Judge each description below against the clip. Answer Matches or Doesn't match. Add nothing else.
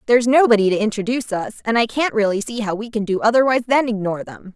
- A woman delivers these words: Matches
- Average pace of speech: Doesn't match